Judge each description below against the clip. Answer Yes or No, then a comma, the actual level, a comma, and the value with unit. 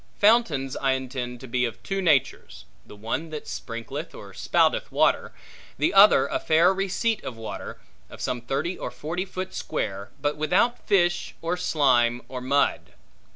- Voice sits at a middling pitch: Yes, medium, 145 Hz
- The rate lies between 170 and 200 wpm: No, average, 160 wpm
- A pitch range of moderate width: No, wide, 6.3 semitones